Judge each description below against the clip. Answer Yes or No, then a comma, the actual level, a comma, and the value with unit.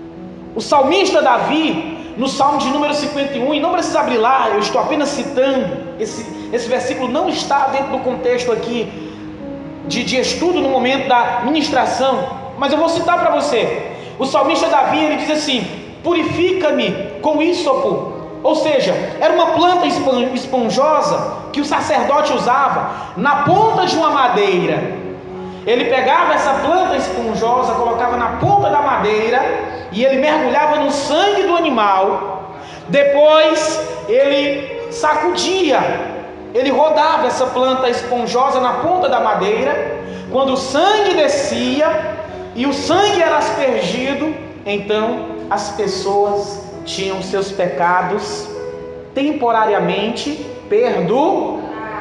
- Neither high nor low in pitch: No, very high, 275 Hz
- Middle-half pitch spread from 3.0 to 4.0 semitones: No, average, 4.5 semitones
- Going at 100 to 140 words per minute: Yes, average, 125 wpm